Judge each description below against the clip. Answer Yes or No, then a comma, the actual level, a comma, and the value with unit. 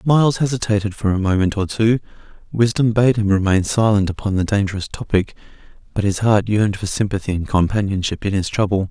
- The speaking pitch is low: Yes, low, 105 Hz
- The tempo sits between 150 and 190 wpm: Yes, average, 180 wpm